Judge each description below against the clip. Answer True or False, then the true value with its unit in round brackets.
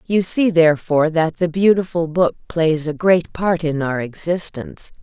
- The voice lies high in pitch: False (165 Hz)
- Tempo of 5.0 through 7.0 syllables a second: False (4.7 syllables/s)